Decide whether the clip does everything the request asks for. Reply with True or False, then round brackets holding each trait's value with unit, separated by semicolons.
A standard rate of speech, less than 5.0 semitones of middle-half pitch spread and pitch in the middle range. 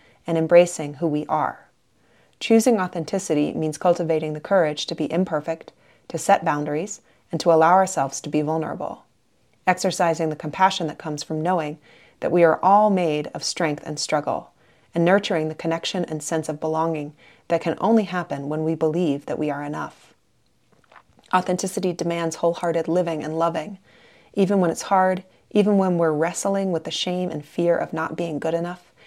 True (170 wpm; 2.6 semitones; 165 Hz)